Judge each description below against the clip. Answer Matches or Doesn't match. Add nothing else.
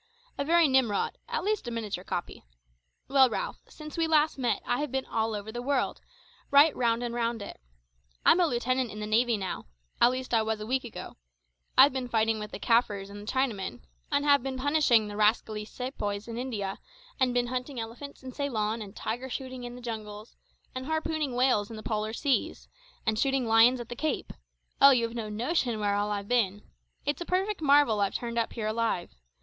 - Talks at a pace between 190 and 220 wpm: Matches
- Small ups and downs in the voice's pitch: Doesn't match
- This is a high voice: Matches